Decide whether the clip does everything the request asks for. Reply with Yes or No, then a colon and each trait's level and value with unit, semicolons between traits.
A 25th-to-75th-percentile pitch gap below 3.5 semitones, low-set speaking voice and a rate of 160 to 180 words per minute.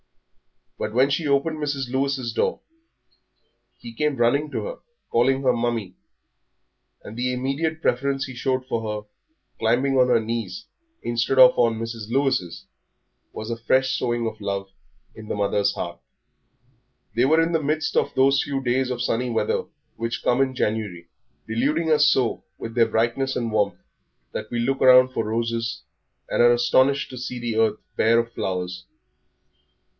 Yes: average, 3.1 semitones; low, 120 Hz; average, 165 wpm